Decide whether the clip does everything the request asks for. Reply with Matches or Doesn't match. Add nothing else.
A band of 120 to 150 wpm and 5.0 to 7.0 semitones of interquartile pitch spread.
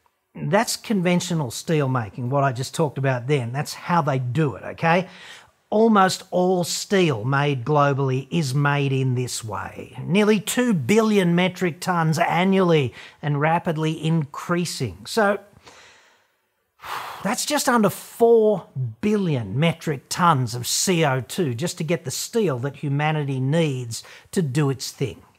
Matches